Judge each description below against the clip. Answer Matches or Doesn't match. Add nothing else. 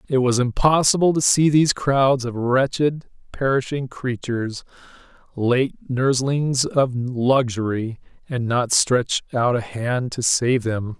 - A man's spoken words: Matches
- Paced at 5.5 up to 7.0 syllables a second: Doesn't match